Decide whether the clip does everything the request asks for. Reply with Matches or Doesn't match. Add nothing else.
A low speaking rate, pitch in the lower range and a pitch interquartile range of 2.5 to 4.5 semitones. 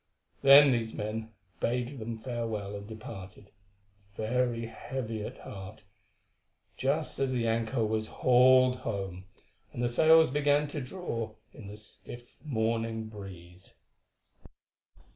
Matches